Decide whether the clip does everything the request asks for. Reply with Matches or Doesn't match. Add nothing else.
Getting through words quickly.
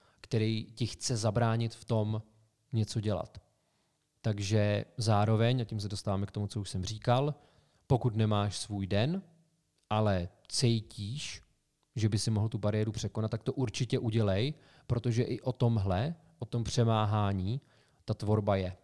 Doesn't match